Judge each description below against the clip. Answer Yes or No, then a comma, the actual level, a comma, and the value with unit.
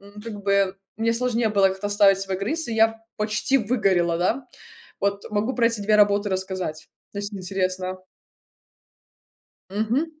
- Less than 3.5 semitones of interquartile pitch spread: Yes, narrow, 2.6 semitones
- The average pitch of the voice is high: Yes, high, 205 Hz